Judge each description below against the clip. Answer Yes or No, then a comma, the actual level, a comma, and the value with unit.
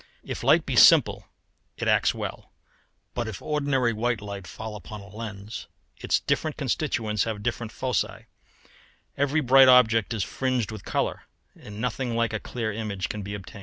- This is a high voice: No, low, 115 Hz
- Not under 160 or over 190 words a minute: Yes, average, 165 wpm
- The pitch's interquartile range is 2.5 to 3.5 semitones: Yes, average, 3.2 semitones